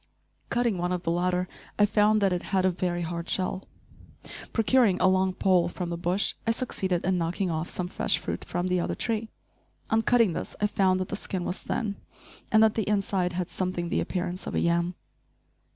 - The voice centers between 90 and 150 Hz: No, medium, 185 Hz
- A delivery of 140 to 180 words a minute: No, fast, 205 wpm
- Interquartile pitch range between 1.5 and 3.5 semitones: Yes, average, 2.7 semitones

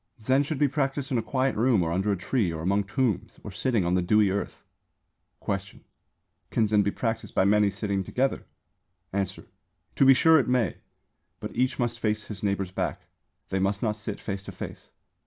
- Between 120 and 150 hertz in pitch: No, low, 105 Hz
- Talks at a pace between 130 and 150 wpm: No, average, 195 wpm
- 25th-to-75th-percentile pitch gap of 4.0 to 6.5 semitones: Yes, average, 4.4 semitones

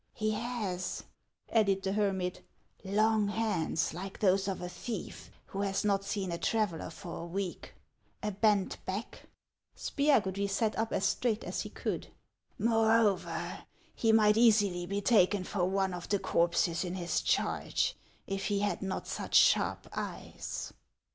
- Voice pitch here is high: Yes, high, 200 Hz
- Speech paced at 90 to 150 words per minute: No, average, 160 wpm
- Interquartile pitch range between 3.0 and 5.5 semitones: No, narrow, 2.5 semitones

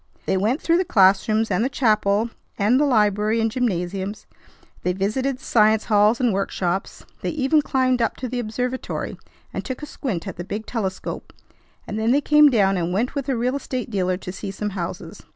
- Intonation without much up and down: No, average, 4.5 semitones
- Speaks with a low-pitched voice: No, high, 220 Hz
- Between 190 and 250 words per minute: Yes, average, 200 wpm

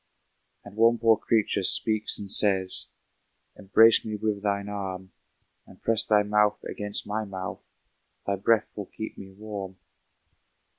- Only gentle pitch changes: Yes, narrow, 1.7 semitones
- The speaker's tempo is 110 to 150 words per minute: Yes, average, 140 wpm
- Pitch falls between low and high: No, low, 105 Hz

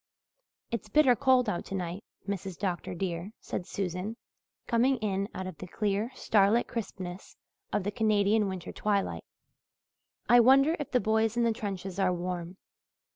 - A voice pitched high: Yes, high, 200 Hz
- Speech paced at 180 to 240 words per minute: No, average, 155 wpm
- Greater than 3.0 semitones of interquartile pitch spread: Yes, average, 3.6 semitones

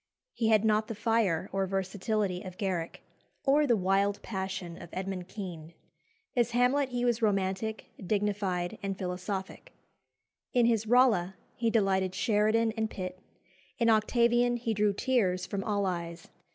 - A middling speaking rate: Yes, average, 145 wpm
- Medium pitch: No, high, 205 Hz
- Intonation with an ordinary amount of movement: Yes, average, 3.4 semitones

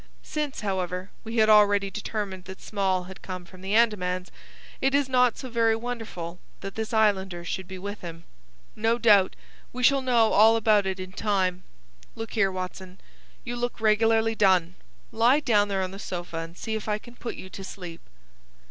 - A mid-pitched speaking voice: No, high, 205 Hz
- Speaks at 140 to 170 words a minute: No, average, 185 wpm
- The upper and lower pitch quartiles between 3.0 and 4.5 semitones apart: Yes, average, 3.3 semitones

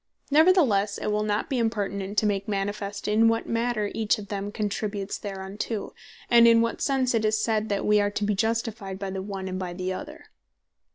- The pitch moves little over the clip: Yes, narrow, 2.3 semitones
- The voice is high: Yes, high, 210 Hz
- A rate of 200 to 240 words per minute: Yes, fast, 205 wpm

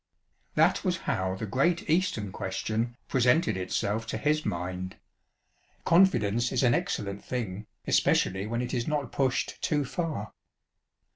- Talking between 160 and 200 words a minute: No, slow, 135 wpm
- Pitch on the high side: No, low, 120 Hz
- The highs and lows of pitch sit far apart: Yes, wide, 6.4 semitones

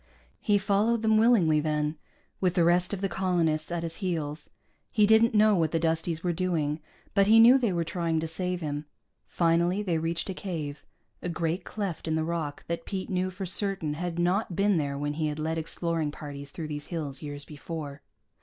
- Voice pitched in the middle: Yes, medium, 170 Hz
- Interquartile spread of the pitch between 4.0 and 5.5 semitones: No, average, 3.4 semitones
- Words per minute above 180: Yes, average, 200 wpm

